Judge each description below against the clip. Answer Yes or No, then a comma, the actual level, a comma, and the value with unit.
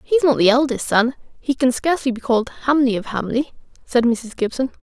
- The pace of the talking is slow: No, average, 200 wpm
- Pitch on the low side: No, very high, 255 Hz